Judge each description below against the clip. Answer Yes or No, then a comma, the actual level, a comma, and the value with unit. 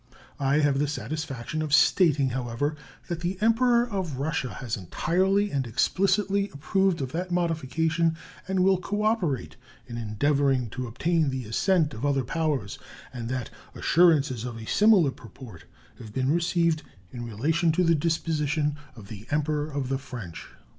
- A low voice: No, medium, 150 Hz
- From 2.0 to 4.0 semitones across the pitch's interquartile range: No, average, 5.2 semitones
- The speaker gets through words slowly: No, average, 155 wpm